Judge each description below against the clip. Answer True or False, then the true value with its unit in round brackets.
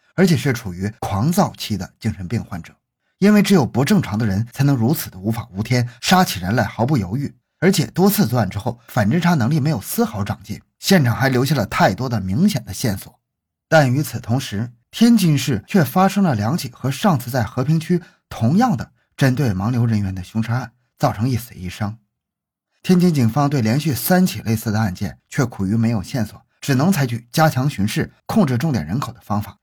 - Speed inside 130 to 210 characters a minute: False (305 characters per minute)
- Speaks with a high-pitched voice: False (125 Hz)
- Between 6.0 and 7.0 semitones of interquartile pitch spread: True (6.4 semitones)